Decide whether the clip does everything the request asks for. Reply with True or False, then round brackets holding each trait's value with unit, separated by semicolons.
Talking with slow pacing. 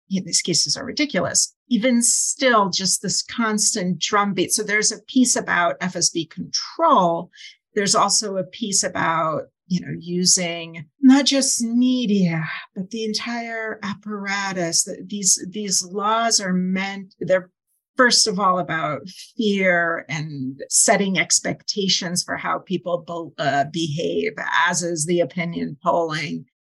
True (130 wpm)